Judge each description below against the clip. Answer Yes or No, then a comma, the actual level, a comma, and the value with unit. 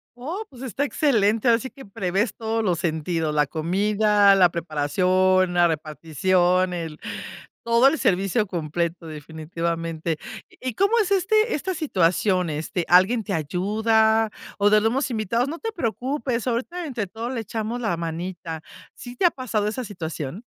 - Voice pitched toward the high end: Yes, high, 200 Hz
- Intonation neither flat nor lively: No, wide, 6.0 semitones